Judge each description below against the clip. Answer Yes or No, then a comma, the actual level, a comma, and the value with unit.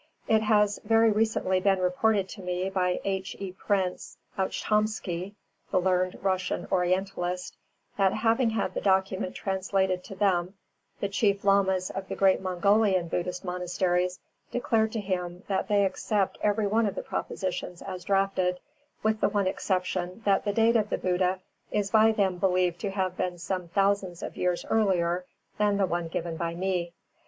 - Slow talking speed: No, average, 165 wpm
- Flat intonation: Yes, narrow, 2.0 semitones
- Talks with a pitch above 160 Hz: Yes, high, 190 Hz